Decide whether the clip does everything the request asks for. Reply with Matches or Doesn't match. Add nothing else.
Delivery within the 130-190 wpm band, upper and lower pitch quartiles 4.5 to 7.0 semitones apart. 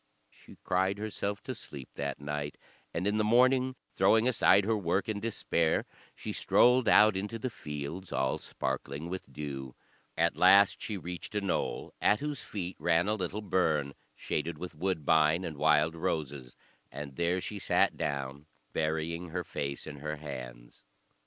Matches